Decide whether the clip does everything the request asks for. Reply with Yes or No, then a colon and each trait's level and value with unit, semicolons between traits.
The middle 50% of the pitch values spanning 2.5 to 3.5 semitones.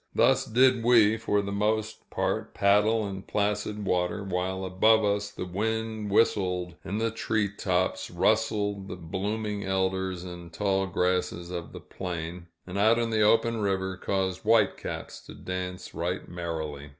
Yes: average, 2.9 semitones